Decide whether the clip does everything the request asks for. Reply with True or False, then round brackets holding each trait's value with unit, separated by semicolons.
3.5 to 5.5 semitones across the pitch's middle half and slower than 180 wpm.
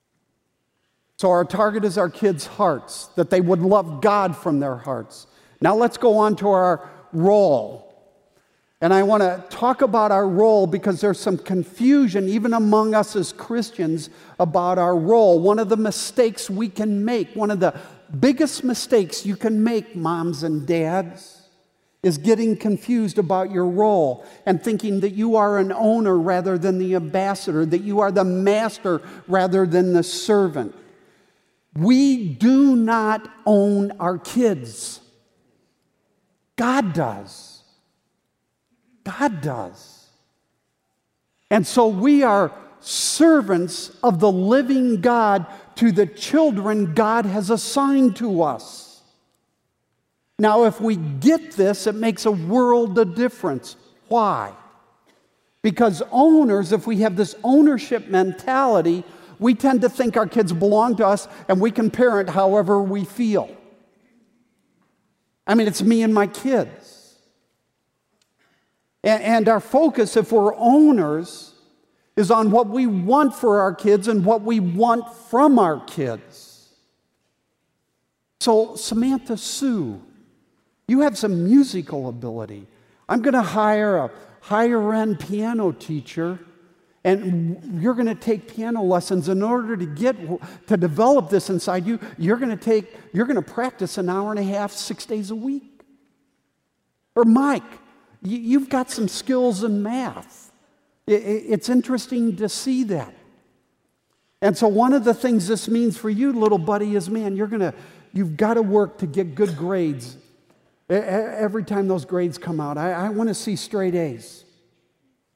True (3.8 semitones; 145 wpm)